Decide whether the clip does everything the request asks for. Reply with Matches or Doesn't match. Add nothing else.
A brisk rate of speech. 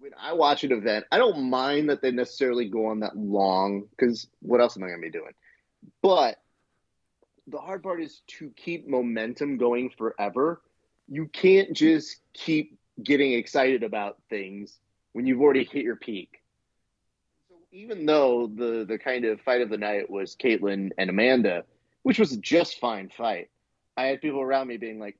Doesn't match